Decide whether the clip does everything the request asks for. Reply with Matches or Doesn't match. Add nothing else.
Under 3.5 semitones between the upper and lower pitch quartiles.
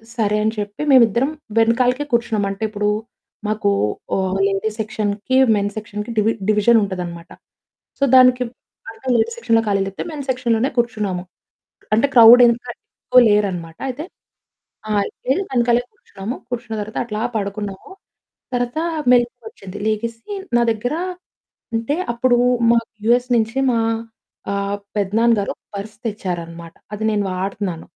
Matches